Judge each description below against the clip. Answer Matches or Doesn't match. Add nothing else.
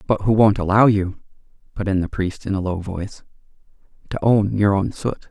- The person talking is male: Matches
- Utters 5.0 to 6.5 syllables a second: Matches